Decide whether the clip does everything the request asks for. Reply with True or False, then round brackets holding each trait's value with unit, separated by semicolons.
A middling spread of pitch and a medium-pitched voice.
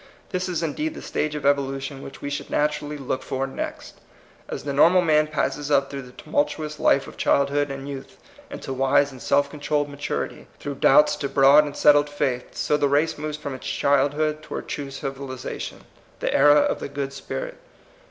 False (1.6 semitones; 145 Hz)